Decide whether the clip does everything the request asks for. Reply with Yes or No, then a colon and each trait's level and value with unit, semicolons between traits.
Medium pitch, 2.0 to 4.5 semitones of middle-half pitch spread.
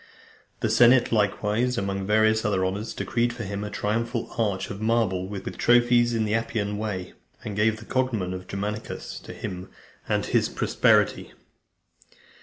No: low, 105 Hz; average, 2.8 semitones